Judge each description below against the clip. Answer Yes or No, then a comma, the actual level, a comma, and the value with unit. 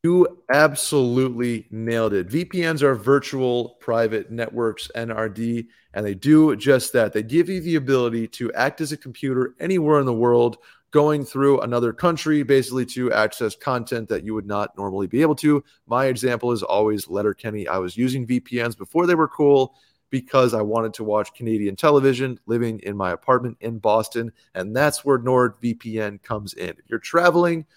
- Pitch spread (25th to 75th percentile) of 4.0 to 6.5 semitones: Yes, average, 4.4 semitones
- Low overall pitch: Yes, low, 125 Hz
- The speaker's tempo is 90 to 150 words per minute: No, average, 175 wpm